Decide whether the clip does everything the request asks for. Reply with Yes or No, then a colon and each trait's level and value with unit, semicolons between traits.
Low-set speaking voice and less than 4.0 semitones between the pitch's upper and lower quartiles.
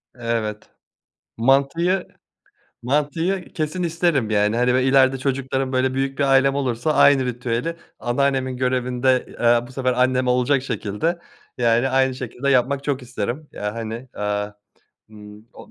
Yes: low, 130 Hz; narrow, 2.6 semitones